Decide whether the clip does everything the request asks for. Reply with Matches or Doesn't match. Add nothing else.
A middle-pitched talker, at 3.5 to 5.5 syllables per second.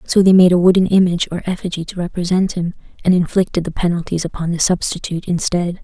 Doesn't match